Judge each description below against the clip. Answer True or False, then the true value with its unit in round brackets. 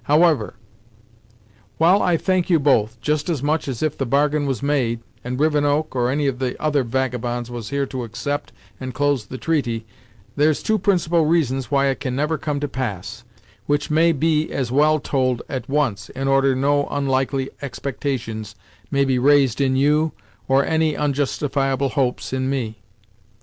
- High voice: False (140 Hz)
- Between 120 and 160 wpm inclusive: False (170 wpm)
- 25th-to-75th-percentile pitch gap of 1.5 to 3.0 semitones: True (2.7 semitones)